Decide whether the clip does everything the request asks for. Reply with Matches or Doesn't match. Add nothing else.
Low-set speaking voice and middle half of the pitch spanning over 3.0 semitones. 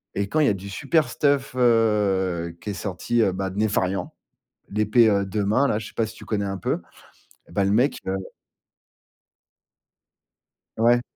Matches